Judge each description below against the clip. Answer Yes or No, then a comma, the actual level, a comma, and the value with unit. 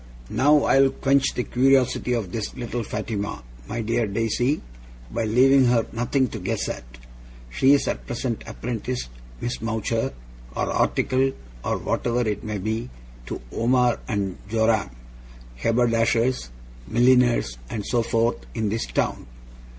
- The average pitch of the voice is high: No, low, 115 Hz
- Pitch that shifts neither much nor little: No, narrow, 2.3 semitones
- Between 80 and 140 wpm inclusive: Yes, slow, 135 wpm